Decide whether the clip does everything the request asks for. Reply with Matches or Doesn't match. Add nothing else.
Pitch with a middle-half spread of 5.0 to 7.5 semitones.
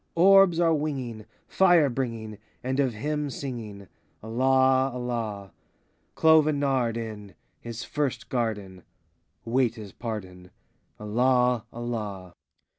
Doesn't match